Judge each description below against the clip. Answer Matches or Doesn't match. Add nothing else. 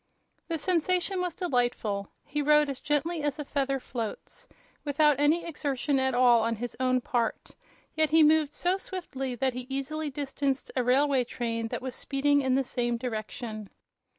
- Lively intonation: Doesn't match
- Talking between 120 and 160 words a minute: Doesn't match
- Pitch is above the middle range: Matches